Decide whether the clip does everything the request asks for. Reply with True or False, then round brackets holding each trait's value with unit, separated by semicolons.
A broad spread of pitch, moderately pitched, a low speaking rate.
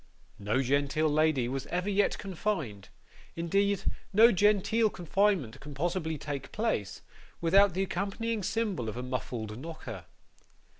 True (7.0 semitones; 170 Hz; 130 wpm)